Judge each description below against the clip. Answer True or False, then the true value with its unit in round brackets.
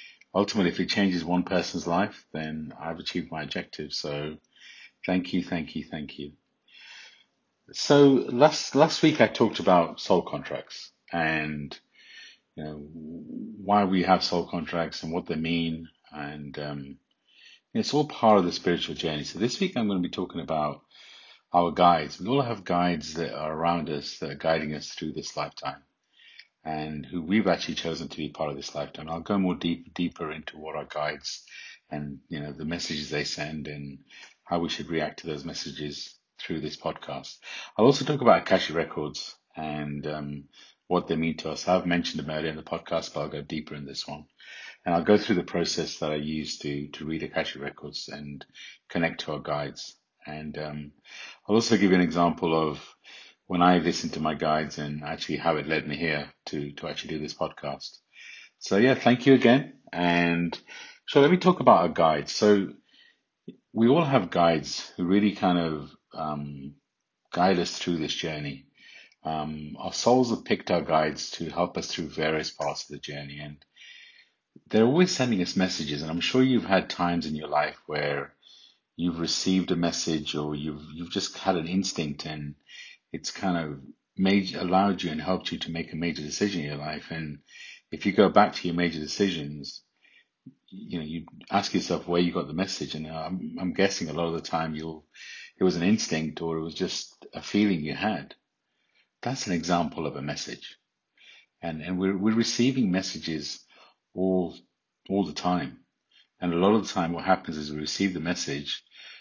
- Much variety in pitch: False (3.5 semitones)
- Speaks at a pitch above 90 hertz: False (80 Hz)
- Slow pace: False (195 wpm)